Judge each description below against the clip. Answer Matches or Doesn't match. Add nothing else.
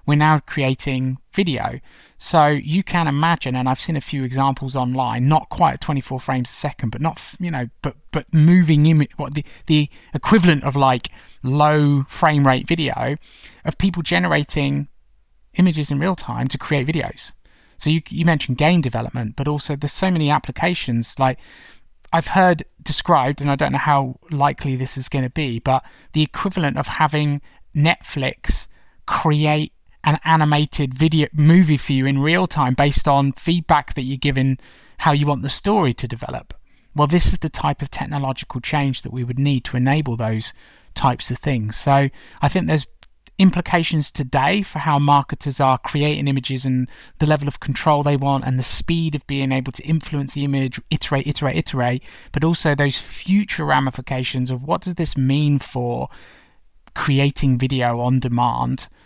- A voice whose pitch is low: Doesn't match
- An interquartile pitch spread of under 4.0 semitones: Matches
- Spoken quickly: Doesn't match